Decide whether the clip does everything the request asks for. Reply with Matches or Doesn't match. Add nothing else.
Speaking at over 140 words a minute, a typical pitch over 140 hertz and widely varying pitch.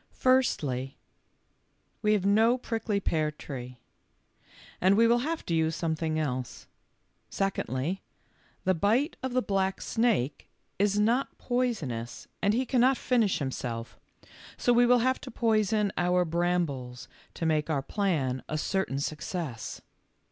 Doesn't match